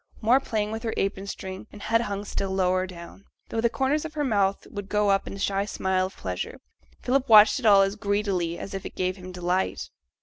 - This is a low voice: No, high, 200 Hz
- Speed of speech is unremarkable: No, fast, 230 wpm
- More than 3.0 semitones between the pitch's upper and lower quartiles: No, average, 2.7 semitones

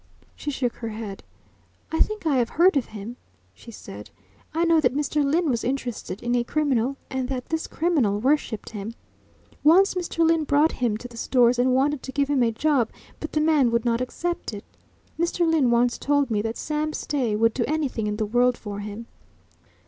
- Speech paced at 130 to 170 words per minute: No, average, 200 wpm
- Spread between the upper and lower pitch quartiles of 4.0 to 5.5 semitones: Yes, average, 4.8 semitones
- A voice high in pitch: Yes, very high, 255 Hz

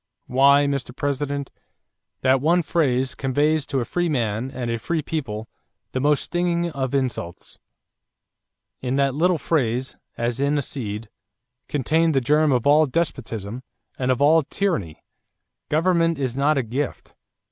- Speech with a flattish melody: No, average, 3.6 semitones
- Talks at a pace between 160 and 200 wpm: No, average, 150 wpm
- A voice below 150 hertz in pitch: Yes, medium, 140 Hz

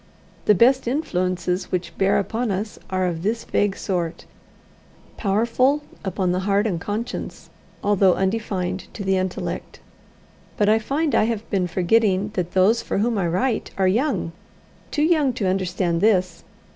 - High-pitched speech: Yes, high, 195 Hz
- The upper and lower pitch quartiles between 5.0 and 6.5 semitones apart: No, average, 3.6 semitones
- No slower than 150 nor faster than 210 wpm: Yes, average, 155 wpm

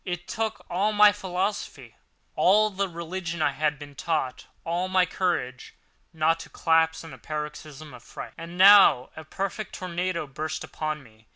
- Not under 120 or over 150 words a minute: No, average, 165 wpm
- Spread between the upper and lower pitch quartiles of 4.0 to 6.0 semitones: No, average, 3.5 semitones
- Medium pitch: Yes, medium, 170 Hz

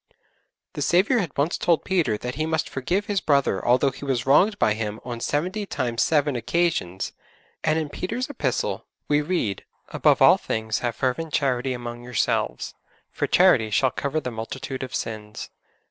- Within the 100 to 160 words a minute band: No, average, 170 wpm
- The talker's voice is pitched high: No, low, 135 Hz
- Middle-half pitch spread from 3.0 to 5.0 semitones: No, wide, 5.4 semitones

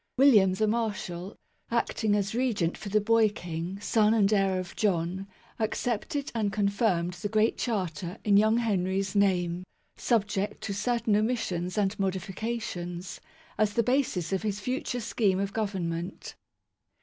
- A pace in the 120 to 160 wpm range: Yes, average, 150 wpm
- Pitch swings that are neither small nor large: Yes, average, 3.0 semitones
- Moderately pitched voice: No, high, 205 Hz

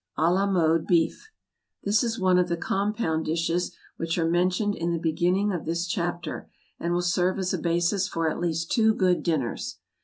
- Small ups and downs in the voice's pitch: Yes, narrow, 2.2 semitones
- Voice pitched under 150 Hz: No, medium, 175 Hz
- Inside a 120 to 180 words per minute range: No, average, 190 wpm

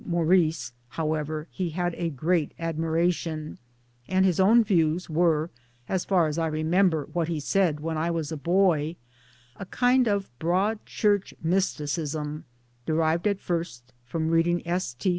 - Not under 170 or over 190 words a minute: No, average, 150 wpm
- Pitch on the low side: No, medium, 165 Hz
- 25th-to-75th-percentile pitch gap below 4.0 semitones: Yes, average, 2.8 semitones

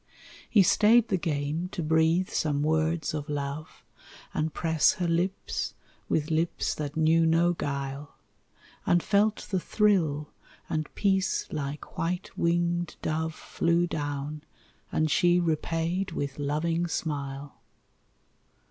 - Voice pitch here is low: No, medium, 160 Hz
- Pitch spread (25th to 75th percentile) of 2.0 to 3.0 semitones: Yes, average, 2.7 semitones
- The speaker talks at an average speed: No, slow, 120 wpm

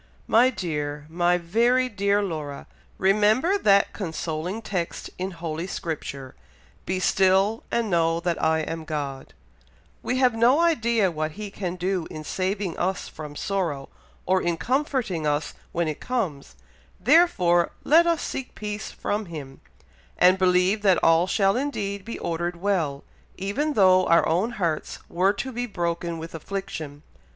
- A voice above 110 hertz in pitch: Yes, medium, 185 Hz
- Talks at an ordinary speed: Yes, average, 150 wpm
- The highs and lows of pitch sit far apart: No, average, 4.5 semitones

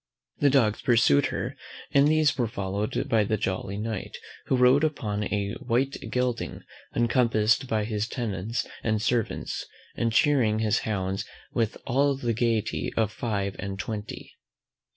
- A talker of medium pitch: No, low, 115 Hz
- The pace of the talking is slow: No, average, 145 wpm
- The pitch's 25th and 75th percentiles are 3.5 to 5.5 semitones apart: No, average, 3.1 semitones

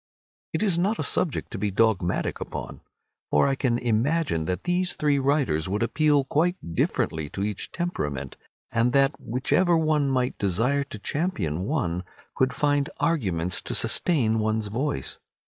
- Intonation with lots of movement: Yes, wide, 7.2 semitones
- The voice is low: Yes, low, 125 Hz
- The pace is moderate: Yes, average, 155 wpm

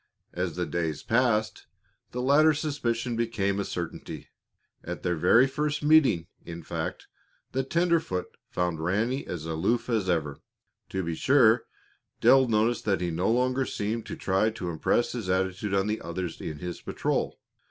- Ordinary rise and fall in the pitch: No, wide, 6.0 semitones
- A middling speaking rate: Yes, average, 160 wpm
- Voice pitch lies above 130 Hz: No, low, 105 Hz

